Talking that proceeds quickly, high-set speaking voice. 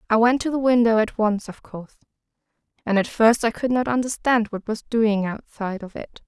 Yes: fast, 210 wpm; high, 225 Hz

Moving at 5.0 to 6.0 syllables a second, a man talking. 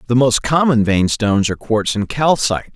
Yes: 5.5 syllables/s; male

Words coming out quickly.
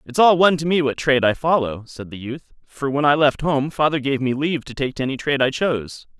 Yes: fast, 270 wpm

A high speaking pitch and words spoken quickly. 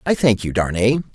No: low, 115 Hz; fast, 210 wpm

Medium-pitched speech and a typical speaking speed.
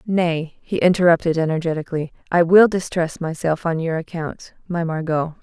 Yes: medium, 165 Hz; average, 145 wpm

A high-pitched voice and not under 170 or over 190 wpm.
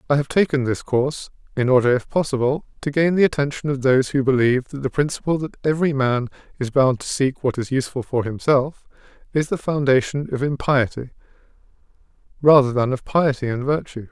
No: low, 135 Hz; average, 185 wpm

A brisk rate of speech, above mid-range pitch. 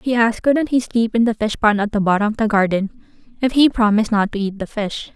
Yes: fast, 270 wpm; high, 220 Hz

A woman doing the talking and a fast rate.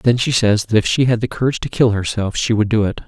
No: male; fast, 315 wpm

